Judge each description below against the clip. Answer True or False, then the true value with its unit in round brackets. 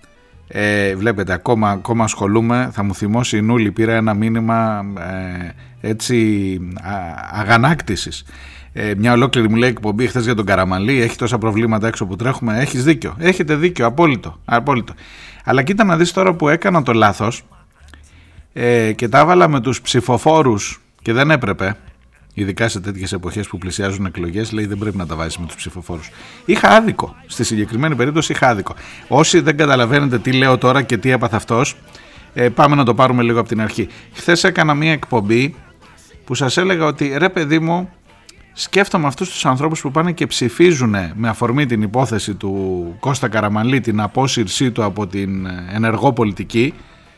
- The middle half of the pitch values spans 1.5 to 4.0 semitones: False (5.0 semitones)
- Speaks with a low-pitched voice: True (115 Hz)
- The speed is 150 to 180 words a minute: True (170 wpm)